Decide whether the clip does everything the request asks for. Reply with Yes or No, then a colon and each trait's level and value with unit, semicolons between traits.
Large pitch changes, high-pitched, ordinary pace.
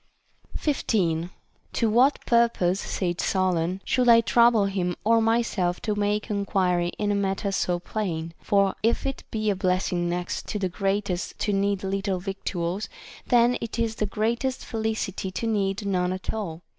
No: average, 3.3 semitones; high, 200 Hz; average, 160 wpm